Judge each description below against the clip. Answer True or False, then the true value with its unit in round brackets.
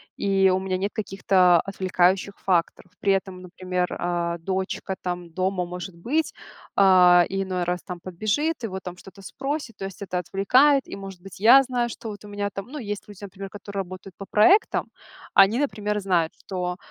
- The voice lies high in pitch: True (195 Hz)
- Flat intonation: True (2.2 semitones)